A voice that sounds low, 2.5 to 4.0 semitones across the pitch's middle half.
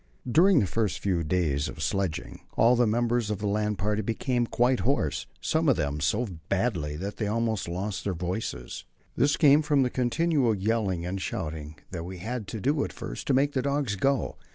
No: low, 105 Hz; wide, 5.5 semitones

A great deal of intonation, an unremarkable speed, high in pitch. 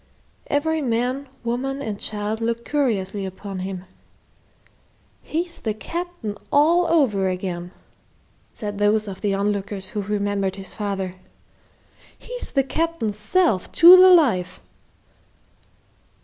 No: wide, 6.5 semitones; slow, 115 wpm; high, 215 Hz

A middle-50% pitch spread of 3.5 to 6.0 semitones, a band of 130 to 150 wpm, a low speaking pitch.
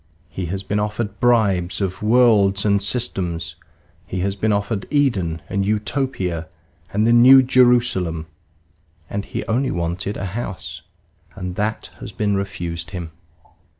Yes: average, 3.8 semitones; average, 140 wpm; low, 100 Hz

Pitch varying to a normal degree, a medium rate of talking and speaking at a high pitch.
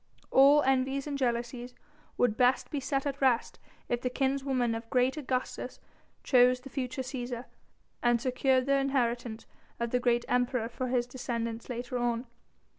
No: narrow, 1.8 semitones; average, 155 wpm; very high, 250 Hz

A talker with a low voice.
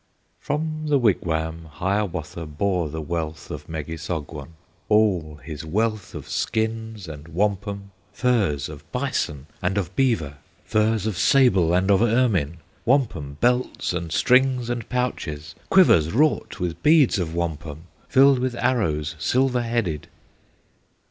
Yes: very low, 95 Hz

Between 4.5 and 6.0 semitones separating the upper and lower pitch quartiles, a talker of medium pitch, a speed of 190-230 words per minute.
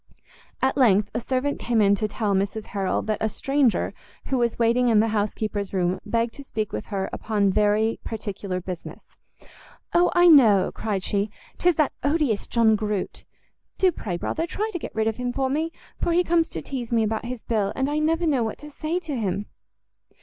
No: wide, 5.4 semitones; high, 225 Hz; fast, 205 wpm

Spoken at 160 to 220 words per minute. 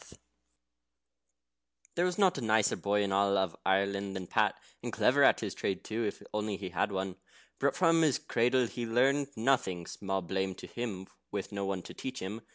Yes: average, 190 wpm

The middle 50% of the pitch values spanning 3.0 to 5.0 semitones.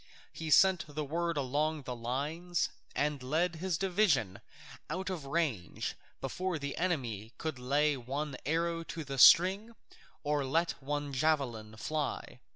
Yes: average, 3.9 semitones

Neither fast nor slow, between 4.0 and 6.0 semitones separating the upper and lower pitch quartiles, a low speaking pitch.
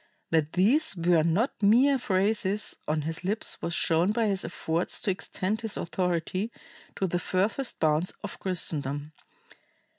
No: average, 145 wpm; average, 4.3 semitones; medium, 185 Hz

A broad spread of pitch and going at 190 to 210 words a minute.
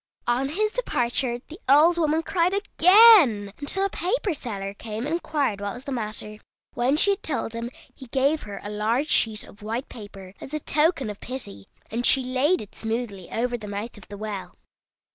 Yes: wide, 6.4 semitones; average, 195 wpm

